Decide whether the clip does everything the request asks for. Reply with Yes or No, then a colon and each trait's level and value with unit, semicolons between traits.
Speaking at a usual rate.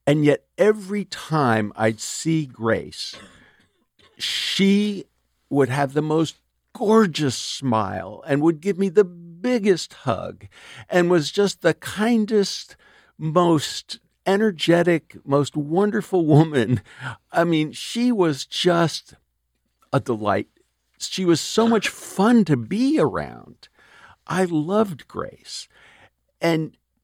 No: slow, 110 wpm